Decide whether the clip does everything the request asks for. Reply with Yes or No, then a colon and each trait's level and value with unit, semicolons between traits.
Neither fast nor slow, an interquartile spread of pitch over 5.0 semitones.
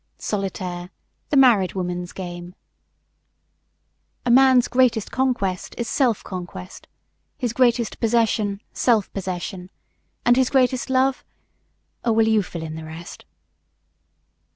No: slow, 115 wpm; wide, 5.4 semitones